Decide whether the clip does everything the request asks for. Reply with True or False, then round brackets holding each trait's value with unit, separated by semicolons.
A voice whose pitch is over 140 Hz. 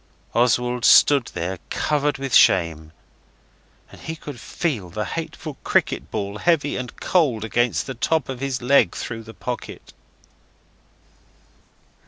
False (125 Hz)